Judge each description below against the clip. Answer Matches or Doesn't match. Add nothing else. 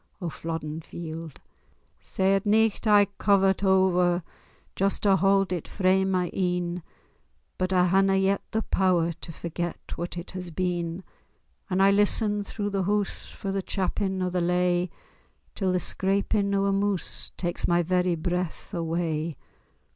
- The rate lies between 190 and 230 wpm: Doesn't match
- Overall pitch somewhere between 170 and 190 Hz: Matches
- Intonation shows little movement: Matches